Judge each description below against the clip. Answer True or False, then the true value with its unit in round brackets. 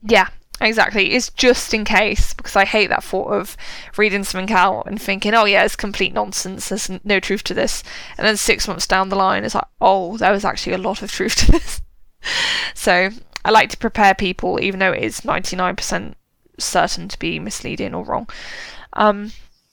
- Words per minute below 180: False (195 wpm)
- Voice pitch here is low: False (200 Hz)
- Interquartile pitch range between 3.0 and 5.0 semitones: False (2.5 semitones)